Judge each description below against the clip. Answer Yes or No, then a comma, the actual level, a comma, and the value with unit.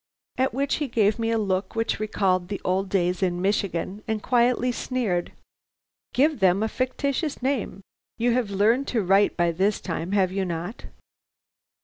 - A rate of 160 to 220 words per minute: Yes, average, 165 wpm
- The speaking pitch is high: Yes, high, 205 Hz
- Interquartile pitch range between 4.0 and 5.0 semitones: Yes, average, 4.5 semitones